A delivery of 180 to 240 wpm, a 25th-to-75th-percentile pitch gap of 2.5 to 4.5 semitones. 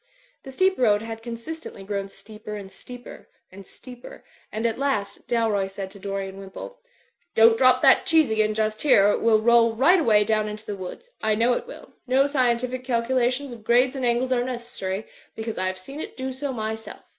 Yes: average, 200 wpm; average, 3.4 semitones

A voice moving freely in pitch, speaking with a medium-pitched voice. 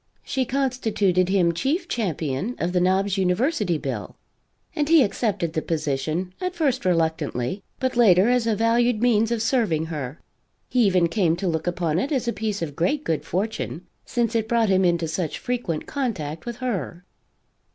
No: wide, 6.2 semitones; high, 195 Hz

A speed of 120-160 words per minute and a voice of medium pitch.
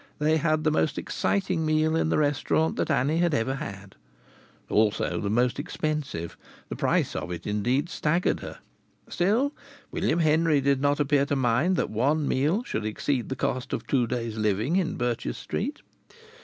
No: average, 170 wpm; medium, 145 Hz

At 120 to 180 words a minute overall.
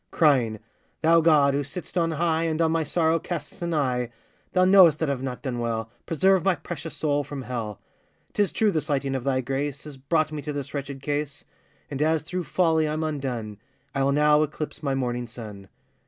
No: average, 200 wpm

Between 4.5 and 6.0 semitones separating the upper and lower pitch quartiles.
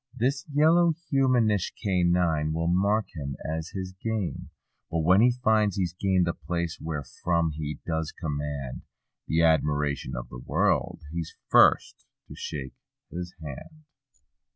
Yes: average, 5.1 semitones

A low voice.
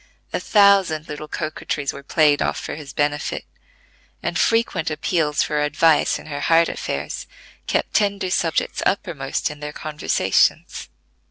No: medium, 155 Hz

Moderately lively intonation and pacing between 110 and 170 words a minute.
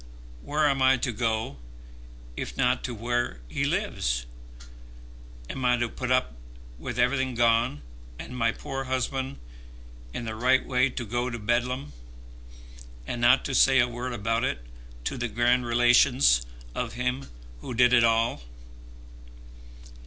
No: narrow, 1.8 semitones; average, 145 wpm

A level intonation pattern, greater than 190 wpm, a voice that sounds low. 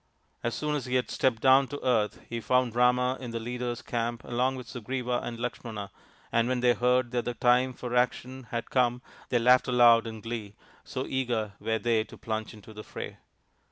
Yes: narrow, 1.6 semitones; average, 200 wpm; low, 120 Hz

